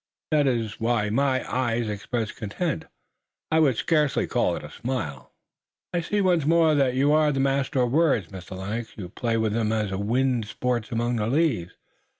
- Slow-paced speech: No, average, 180 wpm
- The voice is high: No, low, 120 Hz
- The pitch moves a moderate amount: Yes, average, 4.6 semitones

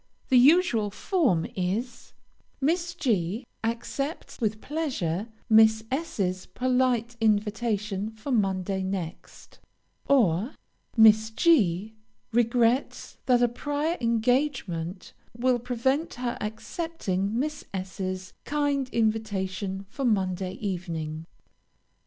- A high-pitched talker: Yes, high, 220 Hz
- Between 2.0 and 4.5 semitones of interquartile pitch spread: No, average, 5.1 semitones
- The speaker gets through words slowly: Yes, slow, 100 wpm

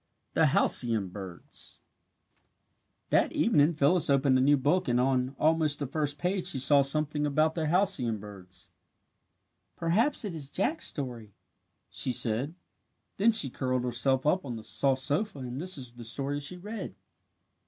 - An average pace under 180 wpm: Yes, average, 155 wpm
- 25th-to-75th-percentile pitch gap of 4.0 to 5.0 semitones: Yes, average, 4.4 semitones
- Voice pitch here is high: No, medium, 140 Hz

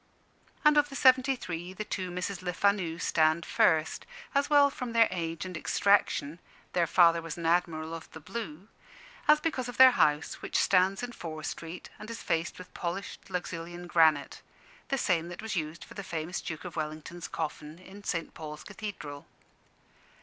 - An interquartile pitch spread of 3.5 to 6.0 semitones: Yes, average, 4.2 semitones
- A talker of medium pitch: Yes, medium, 175 Hz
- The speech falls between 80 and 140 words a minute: No, average, 175 wpm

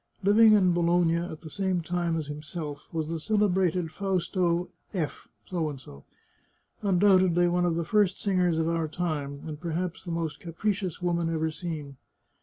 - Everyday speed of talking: Yes, average, 150 wpm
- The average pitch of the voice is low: No, medium, 175 Hz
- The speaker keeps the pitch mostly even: Yes, narrow, 2.3 semitones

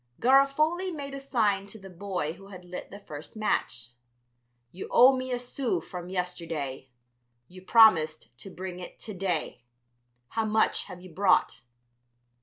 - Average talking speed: Yes, average, 155 wpm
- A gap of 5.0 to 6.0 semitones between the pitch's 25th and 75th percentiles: Yes, wide, 5.4 semitones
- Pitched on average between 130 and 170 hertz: No, high, 195 Hz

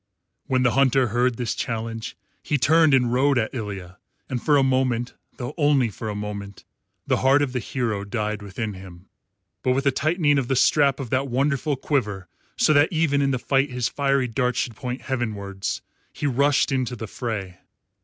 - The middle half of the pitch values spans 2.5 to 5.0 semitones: Yes, average, 3.8 semitones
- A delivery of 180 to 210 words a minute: Yes, average, 190 wpm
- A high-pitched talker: No, low, 125 Hz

